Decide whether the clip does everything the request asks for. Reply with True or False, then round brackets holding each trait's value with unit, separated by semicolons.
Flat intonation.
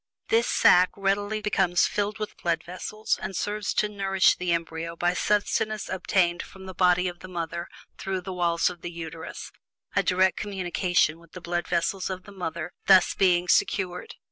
True (2.2 semitones)